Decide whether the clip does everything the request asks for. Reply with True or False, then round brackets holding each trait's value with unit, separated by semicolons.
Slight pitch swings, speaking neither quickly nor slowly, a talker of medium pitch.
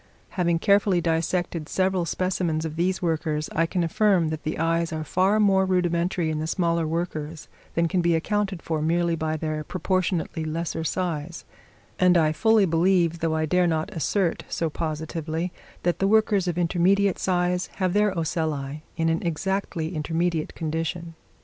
True (2.3 semitones; 160 wpm; 170 Hz)